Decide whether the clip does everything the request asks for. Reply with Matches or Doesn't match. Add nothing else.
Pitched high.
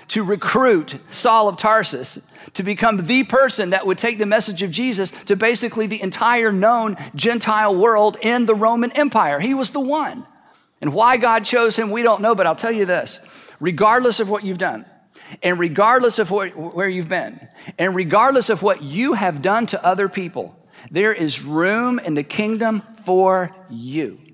Matches